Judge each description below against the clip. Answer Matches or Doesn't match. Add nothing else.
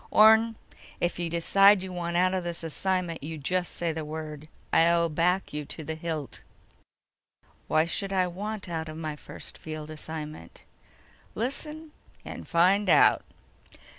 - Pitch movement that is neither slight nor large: Matches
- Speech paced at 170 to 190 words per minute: Doesn't match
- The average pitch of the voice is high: Doesn't match